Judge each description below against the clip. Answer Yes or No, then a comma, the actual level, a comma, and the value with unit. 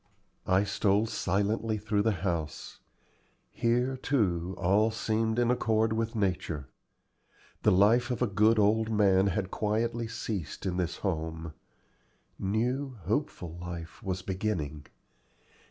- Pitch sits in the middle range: No, low, 105 Hz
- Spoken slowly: Yes, slow, 120 wpm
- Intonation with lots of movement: No, average, 3.5 semitones